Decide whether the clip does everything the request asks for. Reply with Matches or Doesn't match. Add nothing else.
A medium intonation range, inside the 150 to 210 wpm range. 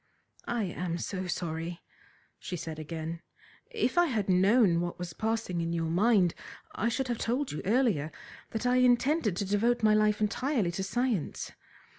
Doesn't match